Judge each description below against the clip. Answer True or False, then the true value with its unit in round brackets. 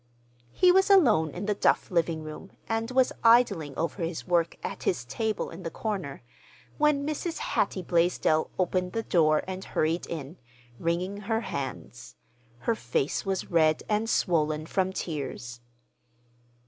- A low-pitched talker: False (180 Hz)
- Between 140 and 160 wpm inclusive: True (145 wpm)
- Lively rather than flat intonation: True (5.7 semitones)